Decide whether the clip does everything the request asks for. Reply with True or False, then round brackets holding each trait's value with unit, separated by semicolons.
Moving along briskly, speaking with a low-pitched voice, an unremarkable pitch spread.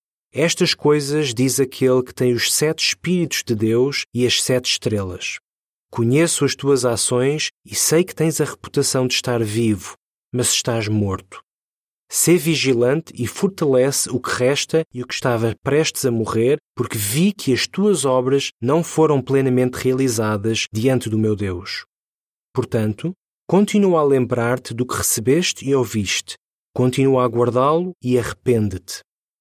False (150 wpm; 130 Hz; 4.2 semitones)